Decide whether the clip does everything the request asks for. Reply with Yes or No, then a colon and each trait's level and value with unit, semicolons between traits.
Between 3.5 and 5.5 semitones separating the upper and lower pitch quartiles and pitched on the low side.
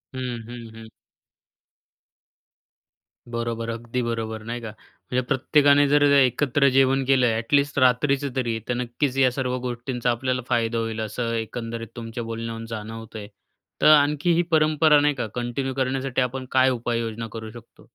No: average, 2.8 semitones; low, 125 Hz